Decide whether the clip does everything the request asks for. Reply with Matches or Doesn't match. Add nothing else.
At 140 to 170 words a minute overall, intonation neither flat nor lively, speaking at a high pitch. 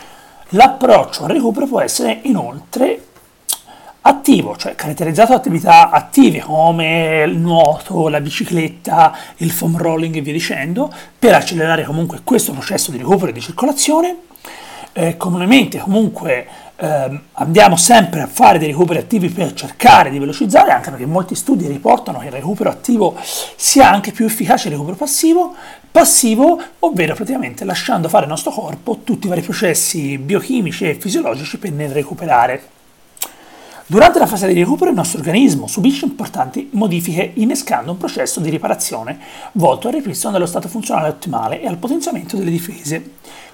Doesn't match